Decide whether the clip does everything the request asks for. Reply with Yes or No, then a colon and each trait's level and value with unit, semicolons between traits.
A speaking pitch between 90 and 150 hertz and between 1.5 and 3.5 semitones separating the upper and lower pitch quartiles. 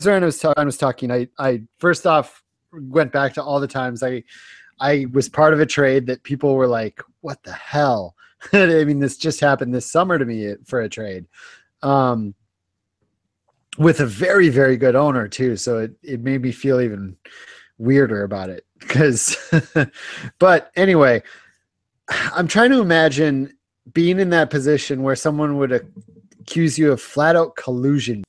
No: low, 135 Hz; average, 4.1 semitones